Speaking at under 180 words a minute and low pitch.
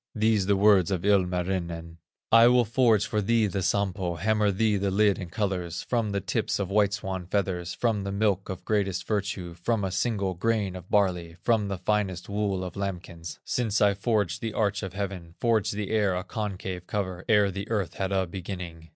No: average, 195 wpm; low, 100 Hz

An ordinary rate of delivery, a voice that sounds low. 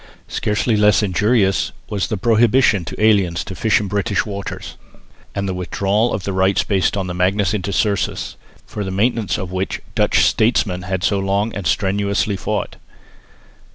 Yes: average, 160 wpm; low, 100 Hz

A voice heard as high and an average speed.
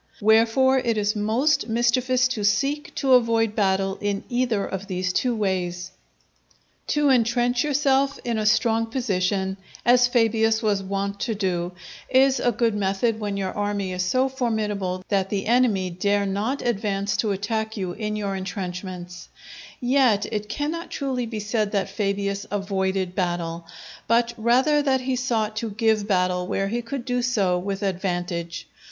Yes: high, 210 Hz; average, 160 wpm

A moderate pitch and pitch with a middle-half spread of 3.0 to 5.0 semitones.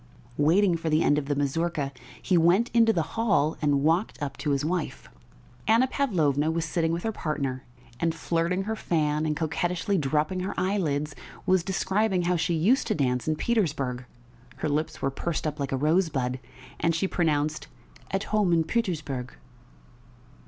Yes: medium, 165 Hz; average, 3.9 semitones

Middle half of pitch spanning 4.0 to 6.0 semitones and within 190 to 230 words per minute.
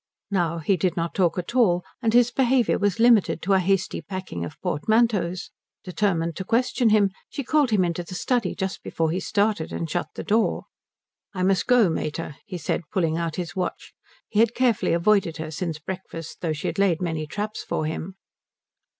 Yes: average, 4.3 semitones; average, 195 wpm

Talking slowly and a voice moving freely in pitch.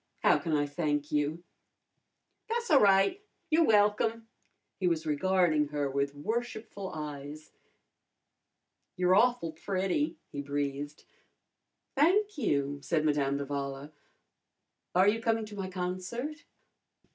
Yes: slow, 110 wpm; wide, 7.3 semitones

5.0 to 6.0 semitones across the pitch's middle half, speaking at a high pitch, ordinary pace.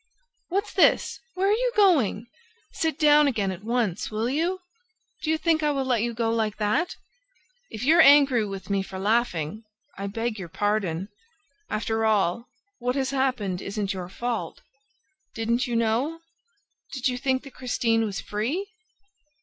Yes: average, 5.3 semitones; high, 235 Hz; average, 160 wpm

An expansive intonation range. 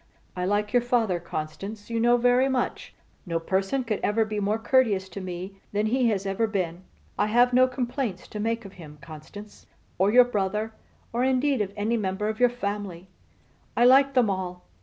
No: average, 4.2 semitones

